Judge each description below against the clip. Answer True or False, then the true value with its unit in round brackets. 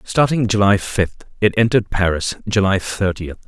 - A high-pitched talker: False (100 Hz)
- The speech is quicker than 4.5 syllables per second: True (5.0 syllables/s)